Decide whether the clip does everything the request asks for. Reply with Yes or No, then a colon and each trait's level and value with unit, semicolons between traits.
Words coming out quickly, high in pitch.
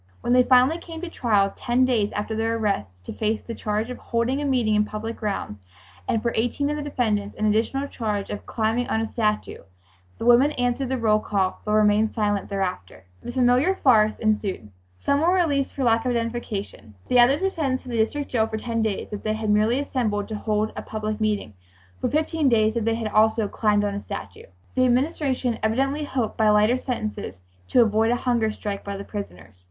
Yes: fast, 210 wpm; high, 225 Hz